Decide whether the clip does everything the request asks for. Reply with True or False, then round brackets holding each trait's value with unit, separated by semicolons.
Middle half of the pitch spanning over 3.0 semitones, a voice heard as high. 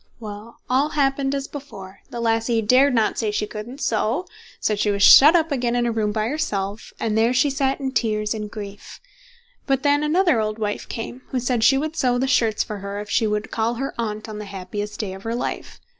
True (4.2 semitones; 230 Hz)